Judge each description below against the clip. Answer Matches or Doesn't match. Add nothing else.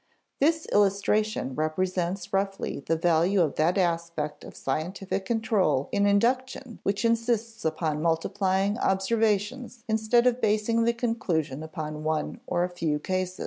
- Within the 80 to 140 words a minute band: Matches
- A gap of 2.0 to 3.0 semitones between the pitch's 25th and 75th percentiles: Doesn't match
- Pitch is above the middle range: Matches